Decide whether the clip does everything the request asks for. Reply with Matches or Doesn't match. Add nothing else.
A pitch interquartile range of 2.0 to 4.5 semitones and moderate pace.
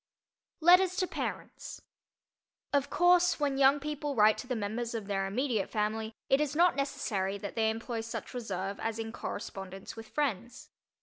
Doesn't match